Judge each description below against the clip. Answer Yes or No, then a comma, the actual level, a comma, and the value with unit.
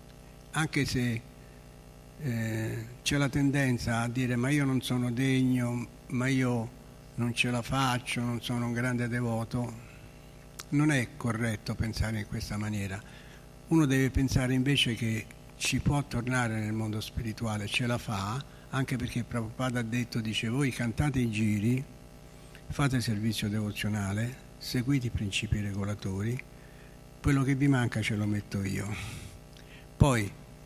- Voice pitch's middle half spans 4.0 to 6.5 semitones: No, average, 3.0 semitones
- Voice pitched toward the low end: Yes, low, 120 Hz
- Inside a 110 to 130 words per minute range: No, average, 140 wpm